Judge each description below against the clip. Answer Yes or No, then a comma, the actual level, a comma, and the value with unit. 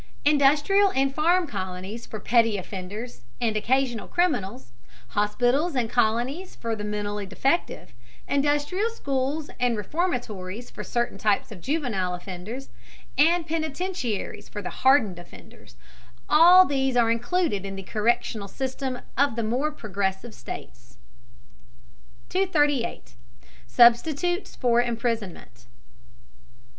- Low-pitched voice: No, high, 240 Hz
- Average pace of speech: No, slow, 110 wpm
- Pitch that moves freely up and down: Yes, wide, 5.9 semitones